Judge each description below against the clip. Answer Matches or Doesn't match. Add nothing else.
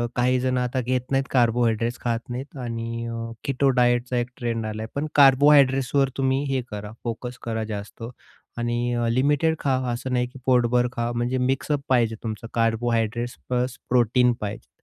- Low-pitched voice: Matches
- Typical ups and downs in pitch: Doesn't match